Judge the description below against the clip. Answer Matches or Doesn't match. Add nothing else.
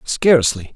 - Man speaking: Matches